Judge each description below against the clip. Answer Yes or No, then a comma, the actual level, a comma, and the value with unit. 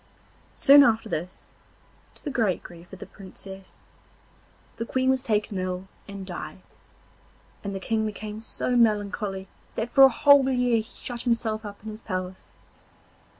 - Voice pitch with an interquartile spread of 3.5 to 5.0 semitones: Yes, average, 3.8 semitones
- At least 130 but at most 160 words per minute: Yes, average, 155 wpm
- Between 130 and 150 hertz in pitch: No, high, 215 Hz